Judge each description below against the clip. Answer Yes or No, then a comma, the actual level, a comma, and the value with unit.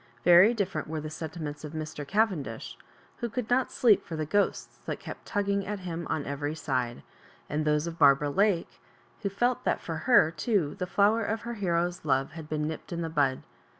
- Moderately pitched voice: Yes, medium, 165 Hz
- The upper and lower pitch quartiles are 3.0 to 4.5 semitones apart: No, average, 5.1 semitones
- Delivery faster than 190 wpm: Yes, average, 200 wpm